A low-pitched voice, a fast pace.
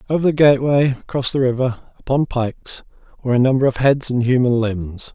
No: low, 130 Hz; average, 185 wpm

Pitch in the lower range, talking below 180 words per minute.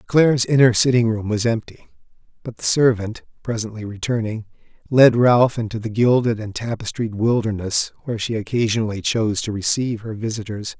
Yes: low, 110 Hz; average, 150 wpm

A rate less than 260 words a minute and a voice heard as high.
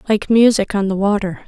Yes: fast, 205 wpm; high, 205 Hz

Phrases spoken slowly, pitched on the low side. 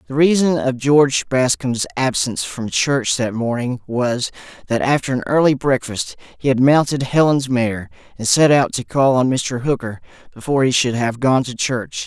No: average, 180 wpm; low, 130 Hz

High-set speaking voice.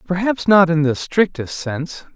No: medium, 170 Hz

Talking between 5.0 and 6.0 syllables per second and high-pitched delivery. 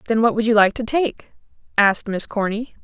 Yes: 5.6 syllables/s; high, 220 Hz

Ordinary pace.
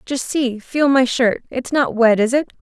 No: fast, 225 wpm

